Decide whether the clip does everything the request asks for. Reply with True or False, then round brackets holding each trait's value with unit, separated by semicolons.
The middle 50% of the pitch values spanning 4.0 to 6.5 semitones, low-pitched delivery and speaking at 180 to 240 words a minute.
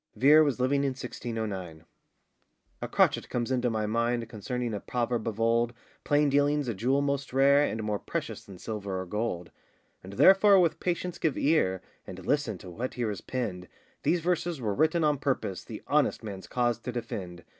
True (5.2 semitones; 120 Hz; 185 wpm)